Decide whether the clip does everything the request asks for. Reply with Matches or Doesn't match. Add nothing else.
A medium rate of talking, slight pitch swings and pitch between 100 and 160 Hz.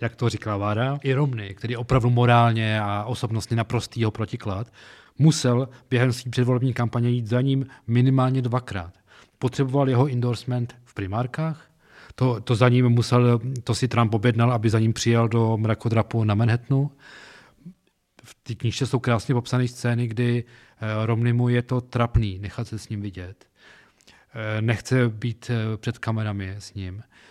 Matches